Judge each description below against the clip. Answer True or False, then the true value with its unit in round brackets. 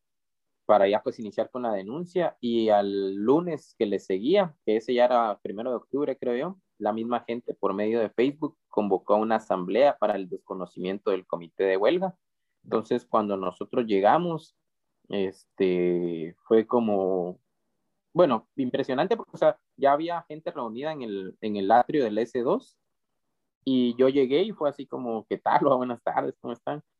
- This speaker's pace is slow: False (170 wpm)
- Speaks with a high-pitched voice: False (120 Hz)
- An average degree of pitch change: False (6.0 semitones)